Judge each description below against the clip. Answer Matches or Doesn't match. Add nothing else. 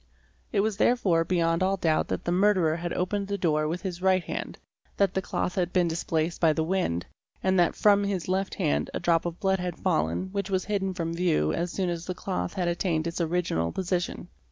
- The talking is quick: Matches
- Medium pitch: Matches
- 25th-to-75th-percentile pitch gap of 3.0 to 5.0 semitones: Doesn't match